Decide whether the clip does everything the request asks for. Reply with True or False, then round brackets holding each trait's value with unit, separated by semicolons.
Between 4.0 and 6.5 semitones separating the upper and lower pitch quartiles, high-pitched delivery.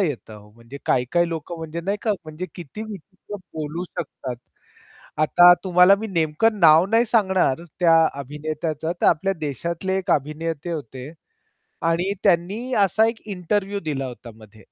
False (4.4 semitones; 165 Hz)